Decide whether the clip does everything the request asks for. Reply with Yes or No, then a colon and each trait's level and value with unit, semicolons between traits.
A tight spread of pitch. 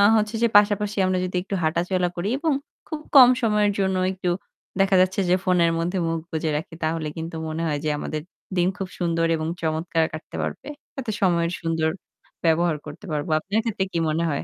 No: average, 3.3 semitones